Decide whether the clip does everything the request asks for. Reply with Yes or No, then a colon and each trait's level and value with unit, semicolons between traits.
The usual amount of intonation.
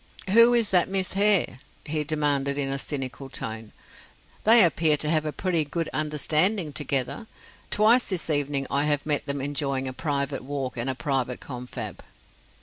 Yes: average, 3.7 semitones